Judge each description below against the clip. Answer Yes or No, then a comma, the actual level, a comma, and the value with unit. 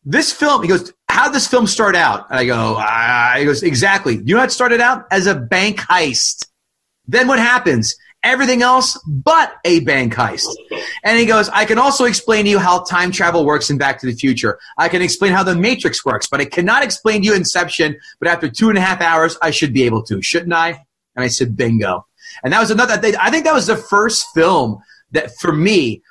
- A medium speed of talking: No, fast, 230 wpm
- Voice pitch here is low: No, high, 190 Hz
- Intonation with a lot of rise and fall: Yes, wide, 7.6 semitones